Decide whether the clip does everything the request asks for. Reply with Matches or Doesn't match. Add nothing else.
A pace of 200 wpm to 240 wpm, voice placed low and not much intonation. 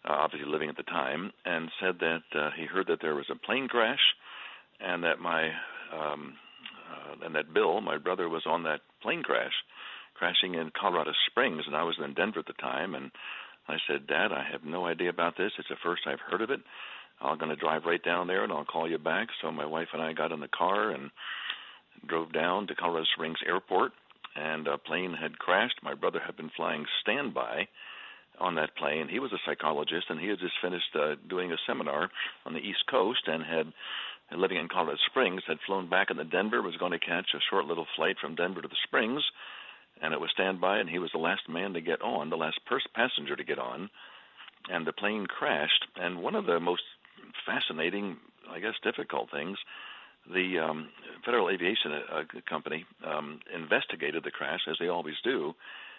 Matches